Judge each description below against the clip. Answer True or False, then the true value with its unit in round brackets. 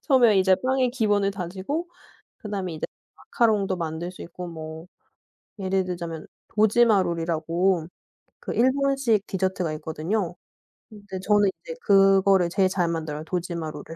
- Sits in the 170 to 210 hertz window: True (190 Hz)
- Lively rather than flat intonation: False (3.7 semitones)